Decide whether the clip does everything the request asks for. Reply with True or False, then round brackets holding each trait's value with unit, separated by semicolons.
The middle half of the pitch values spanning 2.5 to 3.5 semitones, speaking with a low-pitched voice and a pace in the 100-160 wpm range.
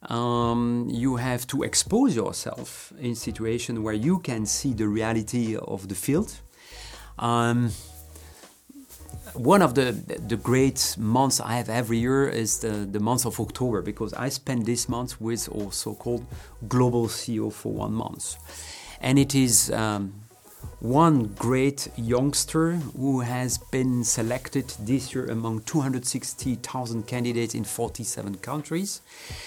True (2.8 semitones; 120 Hz; 135 wpm)